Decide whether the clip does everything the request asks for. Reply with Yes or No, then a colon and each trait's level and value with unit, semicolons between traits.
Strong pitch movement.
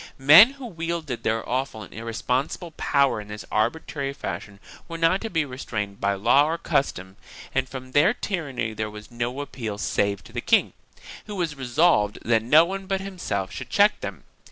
Yes: wide, 7.1 semitones